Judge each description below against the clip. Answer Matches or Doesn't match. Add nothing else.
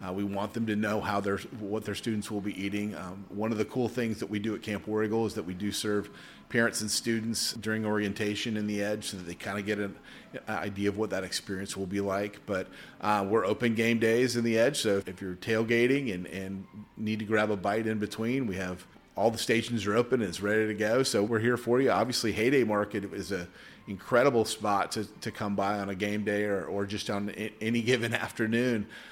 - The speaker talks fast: Matches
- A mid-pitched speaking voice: Doesn't match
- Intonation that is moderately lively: Doesn't match